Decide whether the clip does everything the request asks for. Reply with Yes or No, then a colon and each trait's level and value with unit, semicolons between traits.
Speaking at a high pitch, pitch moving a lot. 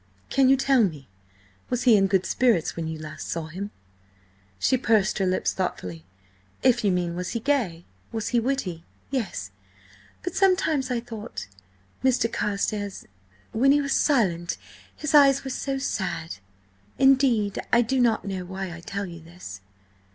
Yes: high, 205 Hz; wide, 7.1 semitones